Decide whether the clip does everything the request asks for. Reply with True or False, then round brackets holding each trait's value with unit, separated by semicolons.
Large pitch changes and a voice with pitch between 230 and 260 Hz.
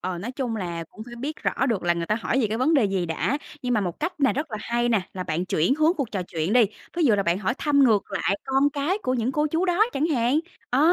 True (6.4 semitones; 240 Hz)